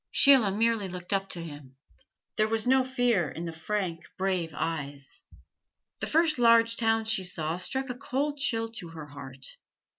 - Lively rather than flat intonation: Yes, wide, 5.9 semitones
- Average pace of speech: Yes, average, 170 wpm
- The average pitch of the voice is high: Yes, high, 200 Hz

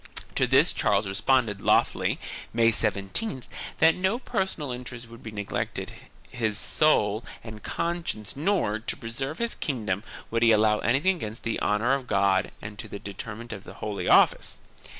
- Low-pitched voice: Yes, low, 115 Hz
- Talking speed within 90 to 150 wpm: No, average, 165 wpm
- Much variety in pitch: No, average, 4.4 semitones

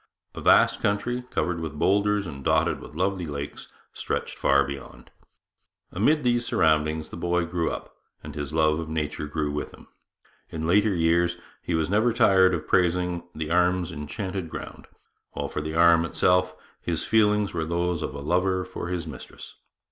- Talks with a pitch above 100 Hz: No, very low, 85 Hz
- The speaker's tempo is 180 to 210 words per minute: No, average, 170 wpm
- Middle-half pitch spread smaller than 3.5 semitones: Yes, average, 3.0 semitones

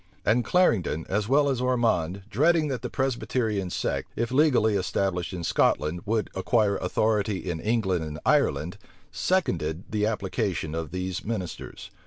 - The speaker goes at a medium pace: Yes, average, 145 wpm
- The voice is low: Yes, low, 105 Hz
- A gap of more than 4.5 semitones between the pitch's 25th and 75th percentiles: Yes, average, 5.1 semitones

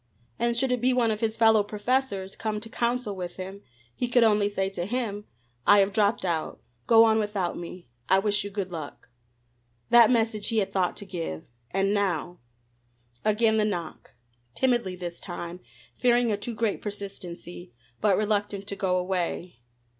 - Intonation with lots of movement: No, average, 3.2 semitones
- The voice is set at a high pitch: Yes, high, 205 Hz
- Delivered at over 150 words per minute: Yes, average, 175 wpm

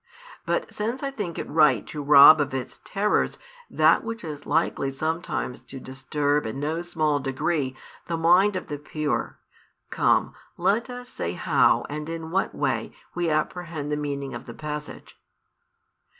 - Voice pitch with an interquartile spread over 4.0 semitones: No, average, 3.4 semitones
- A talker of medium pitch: Yes, medium, 155 Hz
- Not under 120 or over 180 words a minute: Yes, average, 160 wpm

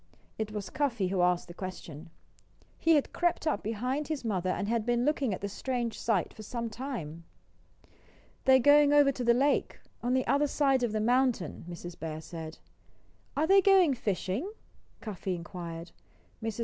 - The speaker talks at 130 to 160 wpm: No, average, 175 wpm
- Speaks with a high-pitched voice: Yes, high, 230 Hz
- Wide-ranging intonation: Yes, wide, 6.8 semitones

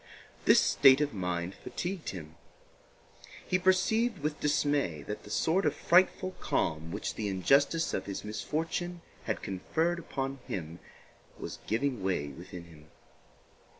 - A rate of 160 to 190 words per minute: No, slow, 135 wpm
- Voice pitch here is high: No, low, 135 Hz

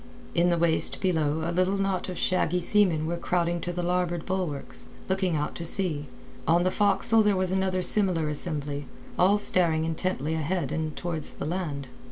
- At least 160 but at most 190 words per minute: Yes, average, 180 wpm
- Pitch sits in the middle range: Yes, medium, 175 Hz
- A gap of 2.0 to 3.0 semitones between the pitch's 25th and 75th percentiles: Yes, average, 2.7 semitones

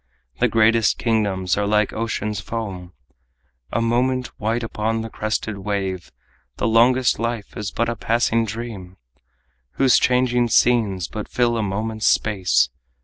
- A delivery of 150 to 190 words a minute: No, average, 140 wpm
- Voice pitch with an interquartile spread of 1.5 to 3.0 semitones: Yes, narrow, 2.4 semitones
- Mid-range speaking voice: No, low, 110 Hz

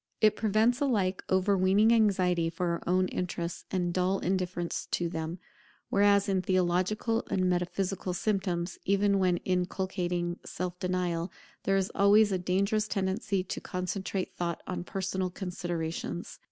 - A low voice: No, medium, 185 Hz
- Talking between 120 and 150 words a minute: Yes, slow, 135 wpm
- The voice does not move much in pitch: Yes, narrow, 2.0 semitones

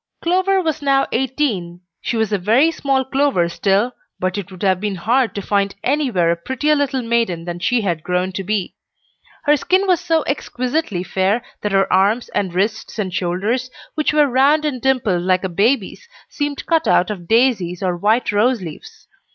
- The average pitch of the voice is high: Yes, high, 220 Hz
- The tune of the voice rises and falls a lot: Yes, wide, 6.5 semitones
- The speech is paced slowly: No, average, 185 wpm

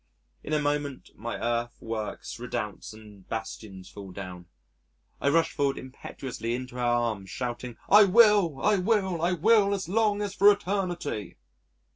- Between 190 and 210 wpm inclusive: No, average, 150 wpm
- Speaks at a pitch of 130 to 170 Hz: Yes, medium, 140 Hz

